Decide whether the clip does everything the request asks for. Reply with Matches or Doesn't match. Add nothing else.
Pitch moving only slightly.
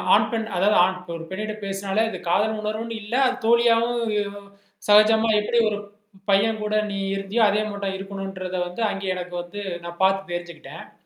Matches